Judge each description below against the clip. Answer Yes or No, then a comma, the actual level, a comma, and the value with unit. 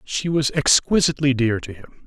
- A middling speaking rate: Yes, average, 175 wpm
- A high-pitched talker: No, low, 135 Hz